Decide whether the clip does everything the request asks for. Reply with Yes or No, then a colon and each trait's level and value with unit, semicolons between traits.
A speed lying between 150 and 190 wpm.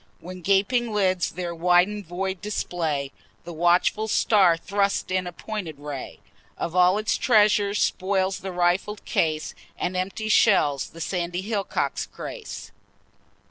No: slow, 135 wpm